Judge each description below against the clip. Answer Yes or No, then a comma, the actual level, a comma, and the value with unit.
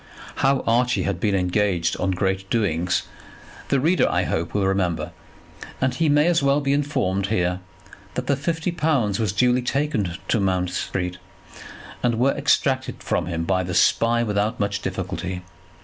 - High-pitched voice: No, low, 105 Hz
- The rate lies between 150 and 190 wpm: Yes, average, 165 wpm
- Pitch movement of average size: No, wide, 6.3 semitones